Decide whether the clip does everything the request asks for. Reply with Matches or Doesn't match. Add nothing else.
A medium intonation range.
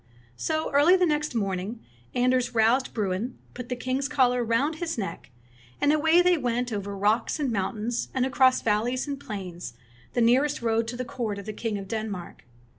Matches